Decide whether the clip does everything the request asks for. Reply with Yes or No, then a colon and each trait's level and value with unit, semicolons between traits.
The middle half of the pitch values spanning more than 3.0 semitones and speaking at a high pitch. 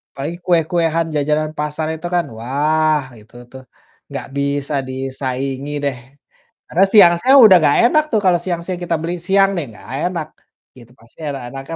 No: average, 4.2 semitones; medium, 155 Hz